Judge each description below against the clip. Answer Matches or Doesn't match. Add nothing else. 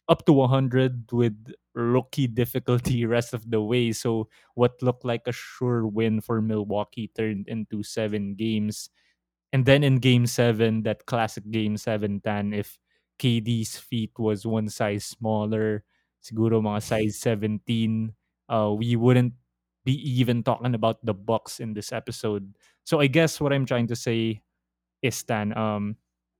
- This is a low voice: Matches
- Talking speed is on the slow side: Doesn't match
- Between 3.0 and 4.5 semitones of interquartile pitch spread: Doesn't match